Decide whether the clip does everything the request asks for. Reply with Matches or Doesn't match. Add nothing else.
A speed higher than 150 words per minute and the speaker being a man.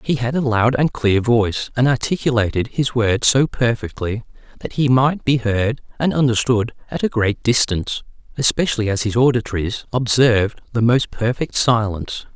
Matches